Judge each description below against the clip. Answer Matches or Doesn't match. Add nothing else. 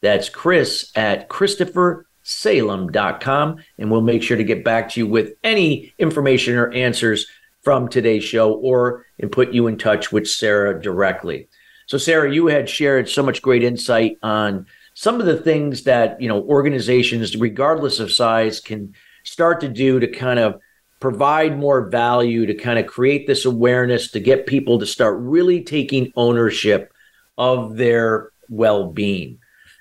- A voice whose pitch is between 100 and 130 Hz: Matches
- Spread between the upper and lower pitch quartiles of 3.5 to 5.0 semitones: Matches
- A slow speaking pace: Doesn't match